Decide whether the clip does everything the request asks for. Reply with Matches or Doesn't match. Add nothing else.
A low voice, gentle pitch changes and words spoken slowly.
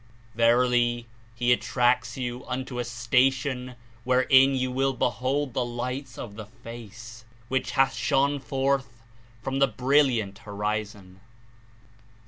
Matches